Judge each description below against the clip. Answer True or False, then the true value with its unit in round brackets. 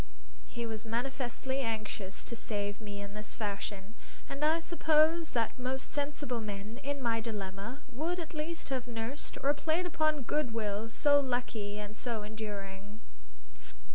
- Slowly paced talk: False (150 wpm)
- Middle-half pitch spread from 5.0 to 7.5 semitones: True (5.3 semitones)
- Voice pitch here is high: True (235 Hz)